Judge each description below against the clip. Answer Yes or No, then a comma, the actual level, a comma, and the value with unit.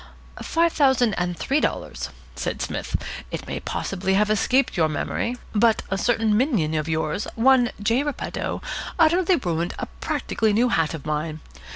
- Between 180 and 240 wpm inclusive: No, average, 160 wpm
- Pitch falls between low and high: No, high, 215 Hz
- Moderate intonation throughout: No, wide, 7.6 semitones